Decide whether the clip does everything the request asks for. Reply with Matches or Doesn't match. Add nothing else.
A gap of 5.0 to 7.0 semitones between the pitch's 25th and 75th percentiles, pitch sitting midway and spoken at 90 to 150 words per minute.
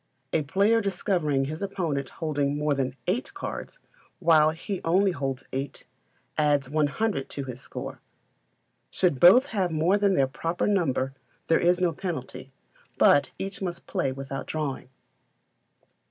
Matches